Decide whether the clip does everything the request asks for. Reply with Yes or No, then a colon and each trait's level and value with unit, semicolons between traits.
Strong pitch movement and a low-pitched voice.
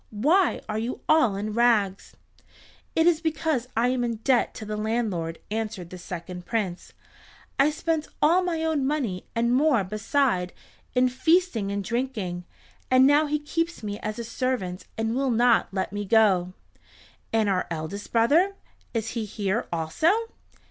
No: wide, 5.8 semitones; high, 230 Hz